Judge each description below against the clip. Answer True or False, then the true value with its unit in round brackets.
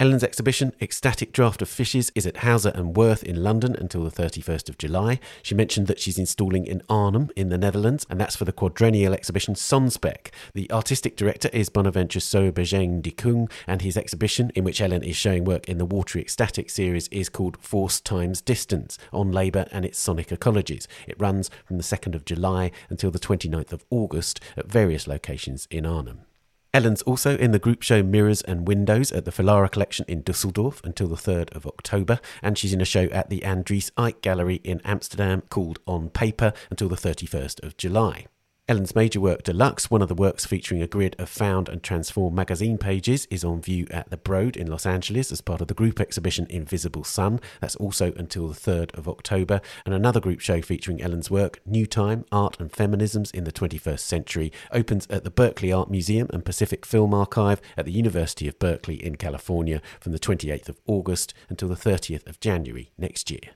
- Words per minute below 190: False (200 wpm)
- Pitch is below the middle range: True (95 Hz)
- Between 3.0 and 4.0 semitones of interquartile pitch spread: True (3.3 semitones)